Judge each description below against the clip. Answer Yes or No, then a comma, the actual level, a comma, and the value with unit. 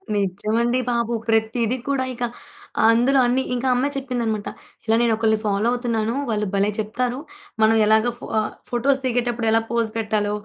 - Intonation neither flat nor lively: No, narrow, 2.2 semitones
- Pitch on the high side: Yes, high, 230 Hz